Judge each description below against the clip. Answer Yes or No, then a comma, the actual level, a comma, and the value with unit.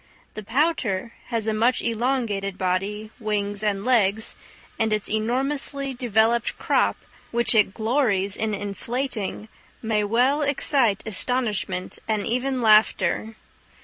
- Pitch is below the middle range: No, high, 220 Hz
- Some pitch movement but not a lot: Yes, average, 3.3 semitones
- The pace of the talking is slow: Yes, slow, 115 wpm